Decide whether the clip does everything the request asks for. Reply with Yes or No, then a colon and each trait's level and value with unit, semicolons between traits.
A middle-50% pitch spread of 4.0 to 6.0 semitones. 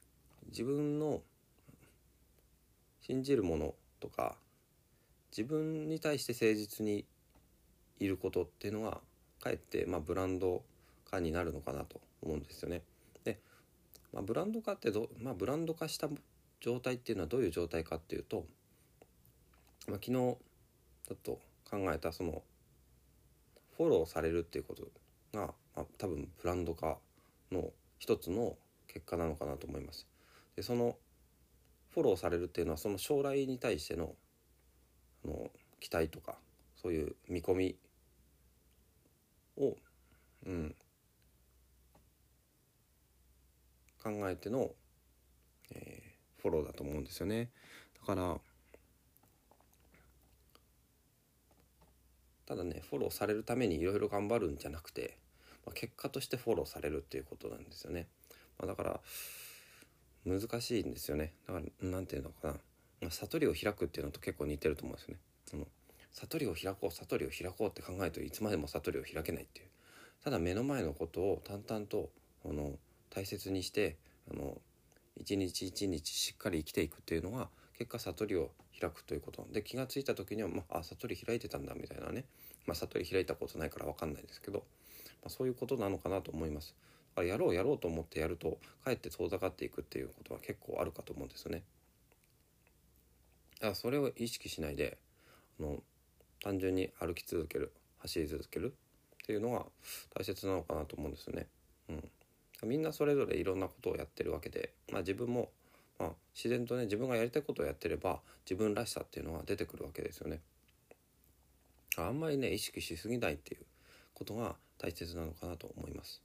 No: wide, 7.2 semitones